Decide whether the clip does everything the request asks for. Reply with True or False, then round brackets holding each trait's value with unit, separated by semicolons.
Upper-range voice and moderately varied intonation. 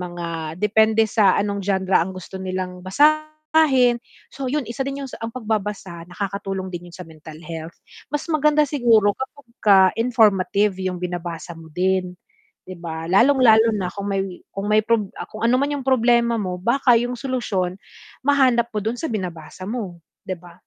True (205 Hz; 5.0 semitones)